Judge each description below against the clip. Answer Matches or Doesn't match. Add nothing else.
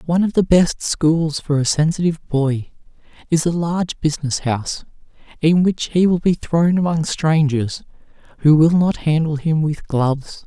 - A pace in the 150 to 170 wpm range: Matches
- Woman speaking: Doesn't match